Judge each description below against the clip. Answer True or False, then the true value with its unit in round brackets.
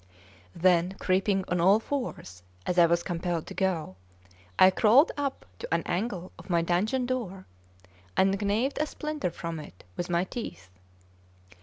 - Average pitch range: True (4.6 semitones)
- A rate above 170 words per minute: False (155 wpm)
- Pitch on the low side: False (185 Hz)